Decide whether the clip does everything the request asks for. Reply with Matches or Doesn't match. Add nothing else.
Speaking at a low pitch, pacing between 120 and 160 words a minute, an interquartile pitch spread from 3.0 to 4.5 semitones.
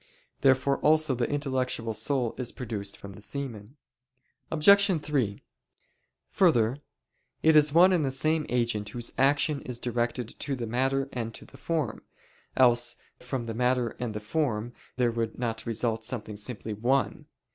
Matches